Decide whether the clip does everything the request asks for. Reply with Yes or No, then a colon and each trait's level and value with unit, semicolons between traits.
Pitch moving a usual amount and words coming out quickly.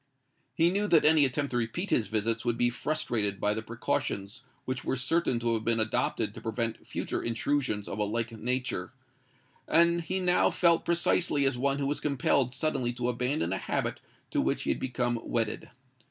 No: average, 4.4 semitones; average, 190 wpm